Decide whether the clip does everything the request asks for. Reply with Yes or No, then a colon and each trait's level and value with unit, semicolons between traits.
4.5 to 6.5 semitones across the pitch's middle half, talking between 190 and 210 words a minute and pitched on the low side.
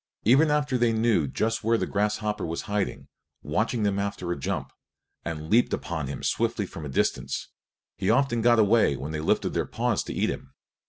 Yes: wide, 5.4 semitones; average, 195 wpm; low, 105 Hz